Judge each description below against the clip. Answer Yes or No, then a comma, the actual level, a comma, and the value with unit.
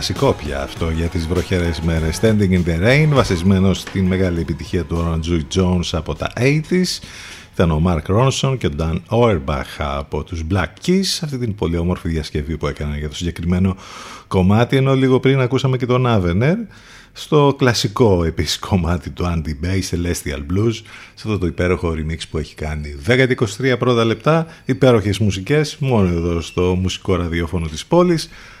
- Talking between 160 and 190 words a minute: Yes, fast, 170 wpm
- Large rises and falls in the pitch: Yes, wide, 6.7 semitones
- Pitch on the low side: Yes, very low, 95 Hz